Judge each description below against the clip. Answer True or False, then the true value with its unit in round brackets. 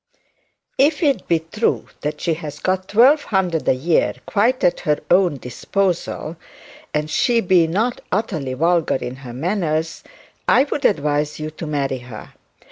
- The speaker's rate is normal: True (155 wpm)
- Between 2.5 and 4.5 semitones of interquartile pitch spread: False (5.1 semitones)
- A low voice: False (165 Hz)